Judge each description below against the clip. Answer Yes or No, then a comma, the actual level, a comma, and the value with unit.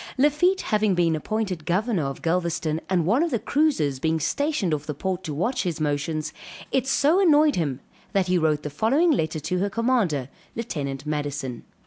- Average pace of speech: Yes, average, 180 wpm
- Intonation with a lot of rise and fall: Yes, wide, 7.7 semitones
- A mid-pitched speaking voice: Yes, medium, 175 Hz